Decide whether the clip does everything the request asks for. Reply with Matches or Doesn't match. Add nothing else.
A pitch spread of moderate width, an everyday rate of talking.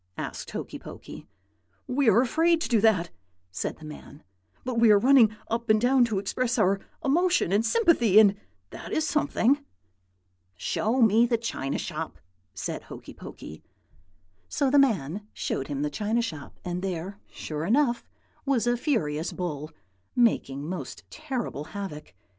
Doesn't match